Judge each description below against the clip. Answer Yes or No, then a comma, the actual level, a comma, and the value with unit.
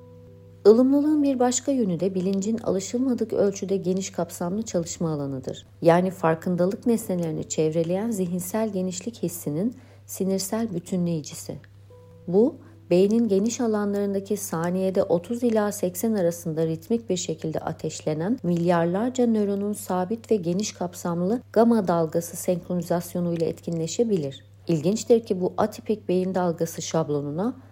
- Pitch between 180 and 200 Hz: Yes, medium, 185 Hz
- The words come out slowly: No, average, 115 wpm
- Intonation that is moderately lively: Yes, average, 4.4 semitones